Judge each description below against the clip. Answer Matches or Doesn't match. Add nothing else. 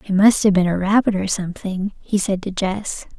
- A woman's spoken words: Matches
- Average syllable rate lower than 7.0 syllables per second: Matches